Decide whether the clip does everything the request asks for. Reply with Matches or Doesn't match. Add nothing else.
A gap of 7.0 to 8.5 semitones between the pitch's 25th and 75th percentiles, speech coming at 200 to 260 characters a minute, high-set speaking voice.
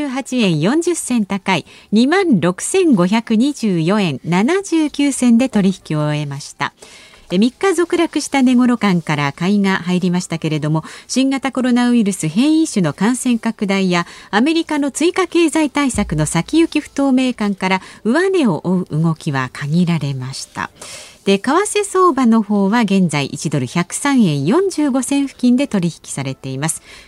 Matches